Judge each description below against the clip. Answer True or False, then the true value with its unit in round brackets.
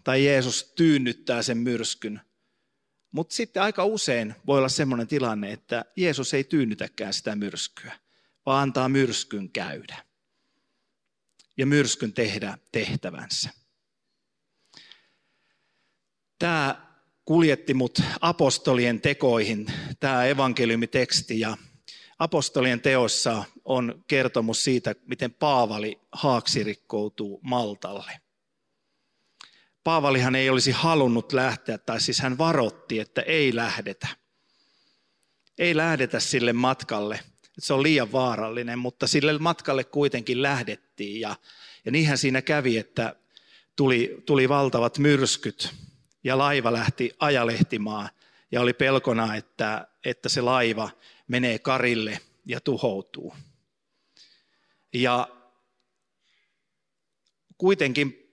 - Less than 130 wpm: True (100 wpm)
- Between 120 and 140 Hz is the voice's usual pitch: True (130 Hz)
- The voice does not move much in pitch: False (3.3 semitones)